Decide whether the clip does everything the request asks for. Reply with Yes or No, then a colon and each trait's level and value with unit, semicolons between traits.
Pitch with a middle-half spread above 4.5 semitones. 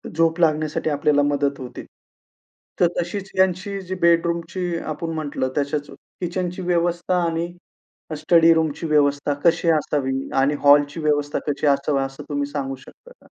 No: average, 3.1 semitones